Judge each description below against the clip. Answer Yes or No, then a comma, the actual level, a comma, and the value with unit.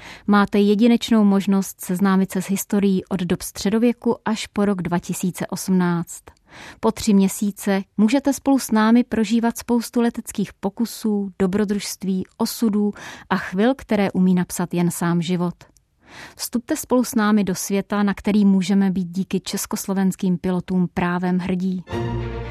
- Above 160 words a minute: No, average, 135 wpm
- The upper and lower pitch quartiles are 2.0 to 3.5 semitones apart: Yes, average, 2.7 semitones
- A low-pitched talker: No, high, 195 Hz